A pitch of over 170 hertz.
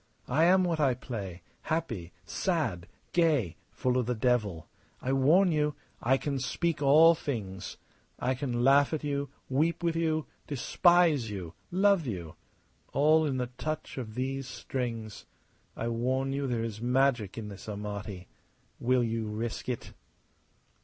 No: low, 130 Hz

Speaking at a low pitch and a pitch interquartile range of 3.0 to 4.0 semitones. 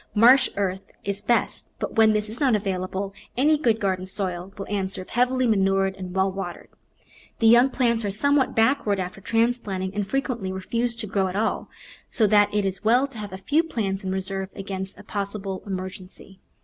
No: high, 200 Hz; average, 3.4 semitones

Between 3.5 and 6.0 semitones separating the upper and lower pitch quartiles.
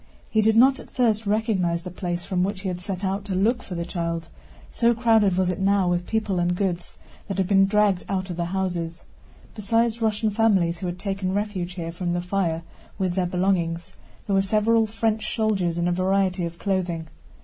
No: average, 3.1 semitones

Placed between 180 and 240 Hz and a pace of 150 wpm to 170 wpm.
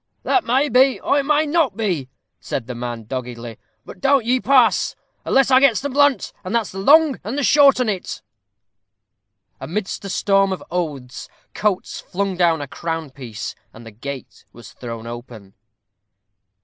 Yes: high, 190 Hz; average, 165 wpm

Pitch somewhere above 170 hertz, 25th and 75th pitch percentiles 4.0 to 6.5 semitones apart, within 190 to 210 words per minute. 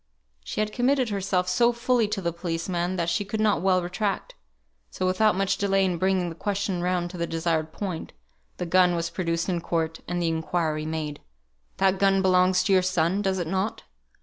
No: medium, 185 Hz; narrow, 2.5 semitones; average, 200 wpm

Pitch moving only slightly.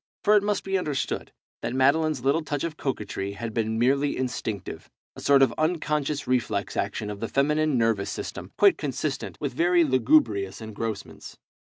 No: wide, 5.6 semitones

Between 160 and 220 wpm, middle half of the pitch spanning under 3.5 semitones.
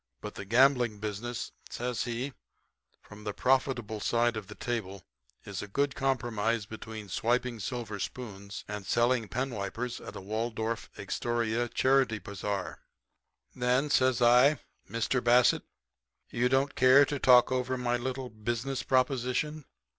No: slow, 135 wpm; average, 2.9 semitones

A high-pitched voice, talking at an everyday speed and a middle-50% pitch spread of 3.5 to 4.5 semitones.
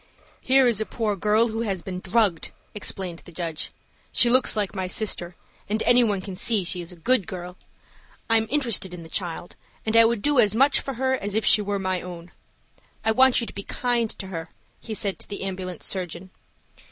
No: high, 205 Hz; fast, 215 wpm; average, 4.0 semitones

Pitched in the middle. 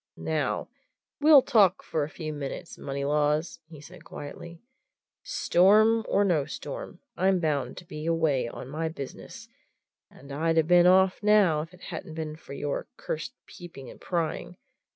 Yes: medium, 160 Hz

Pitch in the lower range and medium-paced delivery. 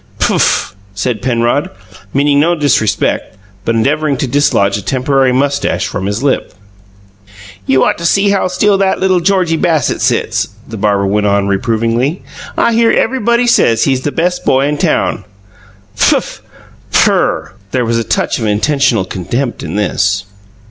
Yes: low, 130 Hz; average, 155 wpm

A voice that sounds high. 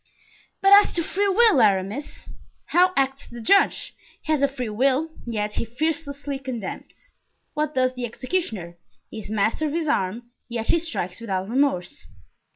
Yes: very high, 265 Hz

